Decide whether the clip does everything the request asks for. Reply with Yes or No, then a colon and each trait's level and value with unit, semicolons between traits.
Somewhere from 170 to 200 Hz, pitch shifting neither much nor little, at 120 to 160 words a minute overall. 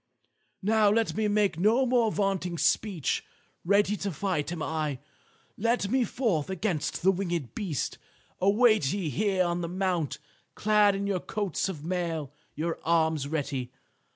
Yes: high, 190 Hz; average, 4.4 semitones; average, 150 wpm